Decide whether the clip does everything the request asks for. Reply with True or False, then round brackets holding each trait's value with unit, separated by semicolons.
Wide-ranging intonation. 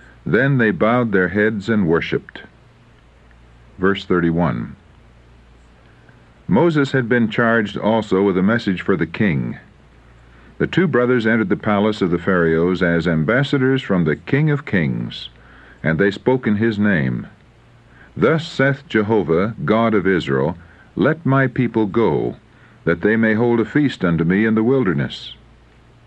True (6.5 semitones)